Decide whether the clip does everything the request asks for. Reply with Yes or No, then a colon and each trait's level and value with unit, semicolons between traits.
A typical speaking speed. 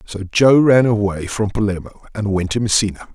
Yes: average, 190 wpm